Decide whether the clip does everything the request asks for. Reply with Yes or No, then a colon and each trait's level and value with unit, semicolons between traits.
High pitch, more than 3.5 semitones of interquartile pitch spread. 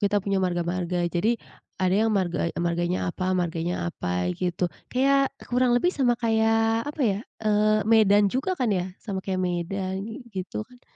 Yes: high, 195 Hz; average, 3.9 semitones